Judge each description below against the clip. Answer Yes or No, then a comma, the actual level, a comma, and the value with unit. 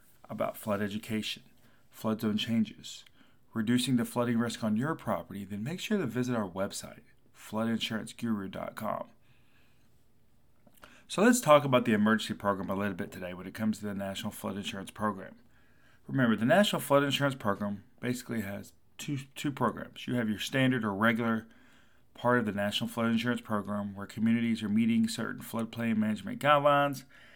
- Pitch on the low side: Yes, low, 115 Hz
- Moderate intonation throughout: Yes, average, 3.0 semitones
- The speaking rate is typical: Yes, average, 160 wpm